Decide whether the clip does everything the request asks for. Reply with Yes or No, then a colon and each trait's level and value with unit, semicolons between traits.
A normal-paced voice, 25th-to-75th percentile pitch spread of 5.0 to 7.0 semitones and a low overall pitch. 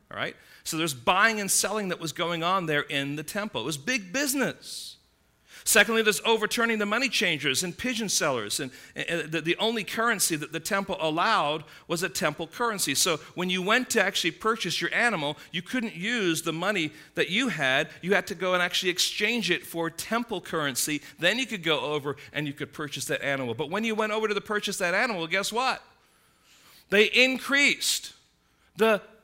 No: average, 195 wpm; average, 5.3 semitones; high, 190 Hz